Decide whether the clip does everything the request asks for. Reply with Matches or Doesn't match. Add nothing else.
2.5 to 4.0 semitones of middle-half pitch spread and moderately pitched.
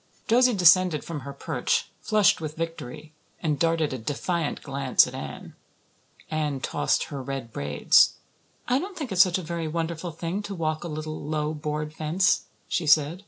Matches